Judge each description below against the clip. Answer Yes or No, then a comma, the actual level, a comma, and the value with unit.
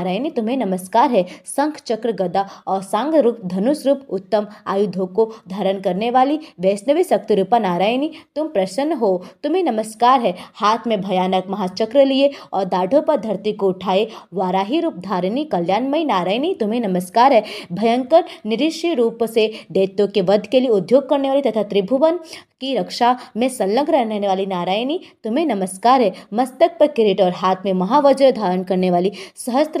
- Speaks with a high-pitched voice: Yes, high, 225 Hz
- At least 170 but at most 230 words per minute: No, average, 130 wpm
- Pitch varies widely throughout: Yes, wide, 6.4 semitones